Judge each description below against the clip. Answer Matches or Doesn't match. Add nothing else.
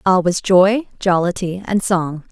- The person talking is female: Matches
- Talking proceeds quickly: Doesn't match